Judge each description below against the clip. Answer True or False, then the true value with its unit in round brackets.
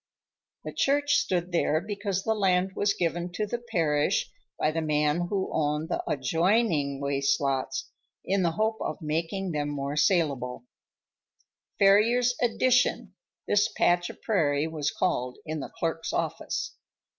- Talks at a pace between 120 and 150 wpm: True (140 wpm)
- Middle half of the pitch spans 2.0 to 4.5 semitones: False (5.3 semitones)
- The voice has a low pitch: False (170 Hz)